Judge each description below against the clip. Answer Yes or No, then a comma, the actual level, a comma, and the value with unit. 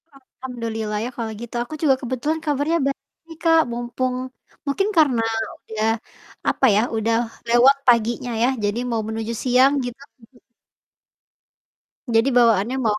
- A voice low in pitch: No, high, 245 Hz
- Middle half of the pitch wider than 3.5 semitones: No, average, 3.2 semitones